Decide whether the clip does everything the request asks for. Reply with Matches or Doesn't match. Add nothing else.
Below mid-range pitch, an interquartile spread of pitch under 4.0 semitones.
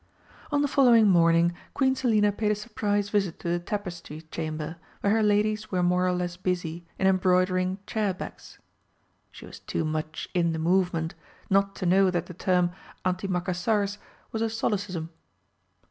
Doesn't match